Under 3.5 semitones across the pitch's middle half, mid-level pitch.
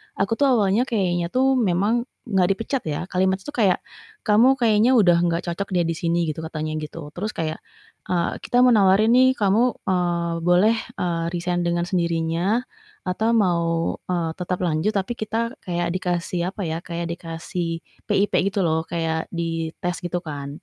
No: average, 3.8 semitones; medium, 180 Hz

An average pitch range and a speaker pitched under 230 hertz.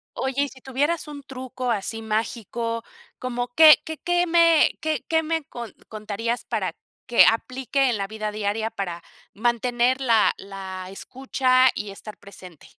No: average, 4.0 semitones; high, 240 Hz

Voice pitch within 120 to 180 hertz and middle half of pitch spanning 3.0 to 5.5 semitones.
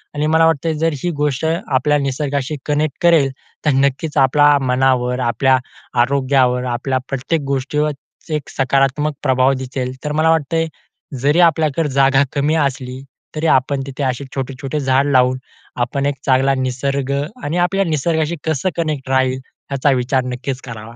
No: medium, 140 Hz; narrow, 2.6 semitones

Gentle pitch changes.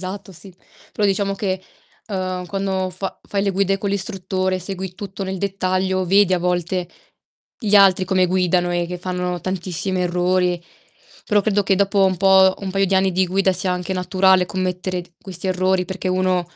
Yes: narrow, 1.2 semitones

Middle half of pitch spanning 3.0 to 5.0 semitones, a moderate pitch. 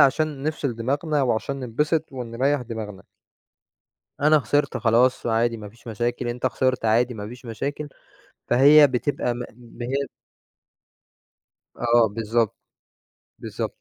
No: average, 3.4 semitones; low, 125 Hz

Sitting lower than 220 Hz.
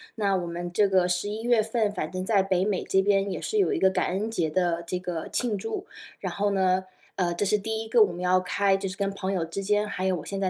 Yes: high, 195 Hz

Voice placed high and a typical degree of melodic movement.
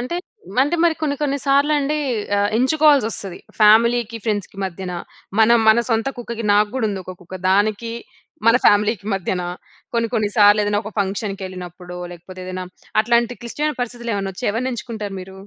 Yes: high, 215 Hz; average, 3.6 semitones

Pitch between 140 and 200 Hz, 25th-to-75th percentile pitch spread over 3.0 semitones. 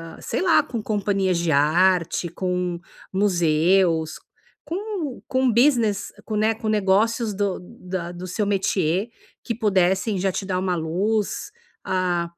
Yes: high, 190 Hz; average, 3.6 semitones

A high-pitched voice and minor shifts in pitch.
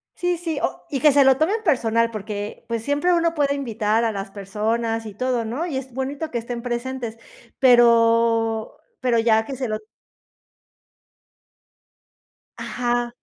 No: high, 240 Hz; average, 3.4 semitones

